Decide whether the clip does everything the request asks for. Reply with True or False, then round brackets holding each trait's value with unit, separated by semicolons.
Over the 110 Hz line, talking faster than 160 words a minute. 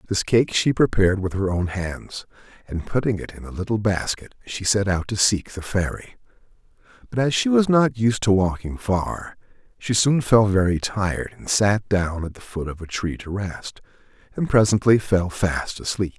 False (100 Hz; 195 wpm)